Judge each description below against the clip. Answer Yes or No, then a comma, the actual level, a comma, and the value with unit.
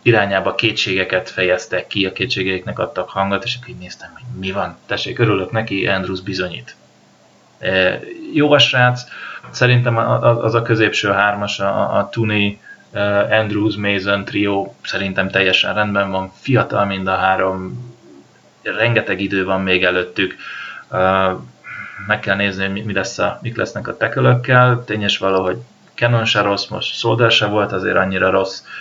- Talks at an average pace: Yes, average, 145 wpm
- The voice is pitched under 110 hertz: Yes, low, 100 Hz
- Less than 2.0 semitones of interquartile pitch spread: No, average, 2.9 semitones